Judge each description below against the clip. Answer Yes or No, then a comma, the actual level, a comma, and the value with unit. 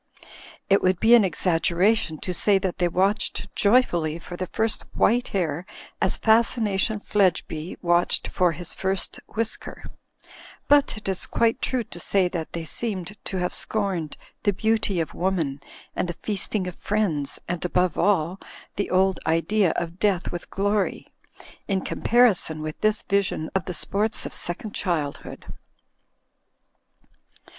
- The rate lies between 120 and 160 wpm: Yes, average, 150 wpm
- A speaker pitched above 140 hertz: Yes, high, 190 Hz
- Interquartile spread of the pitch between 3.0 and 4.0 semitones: Yes, average, 3.4 semitones